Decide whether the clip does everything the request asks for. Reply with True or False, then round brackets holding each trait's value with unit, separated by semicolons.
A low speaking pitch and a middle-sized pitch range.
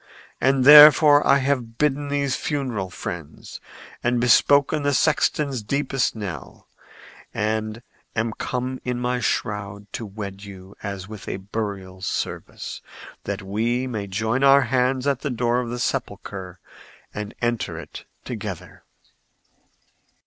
True (120 Hz; 4.9 semitones)